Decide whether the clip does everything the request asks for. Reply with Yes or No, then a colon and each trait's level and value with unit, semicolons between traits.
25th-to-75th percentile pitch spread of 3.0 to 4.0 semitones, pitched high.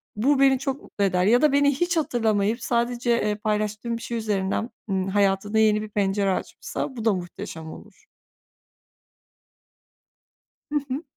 Yes: average, 3.6 semitones; high, 220 Hz